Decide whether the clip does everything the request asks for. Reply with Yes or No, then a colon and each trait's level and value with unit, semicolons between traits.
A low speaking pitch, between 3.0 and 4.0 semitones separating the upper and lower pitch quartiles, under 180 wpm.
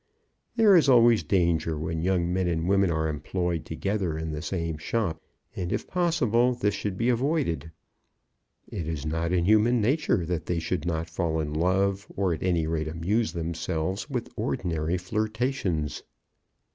No: very low, 90 Hz; average, 4.9 semitones; average, 160 wpm